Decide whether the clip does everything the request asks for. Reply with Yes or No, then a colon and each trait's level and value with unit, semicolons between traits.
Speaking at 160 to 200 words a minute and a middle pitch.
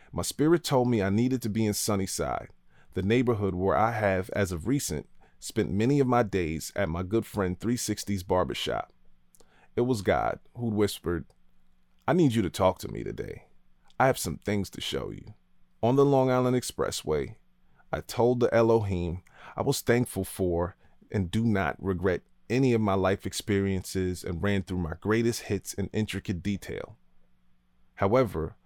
No: average, 170 wpm; low, 100 Hz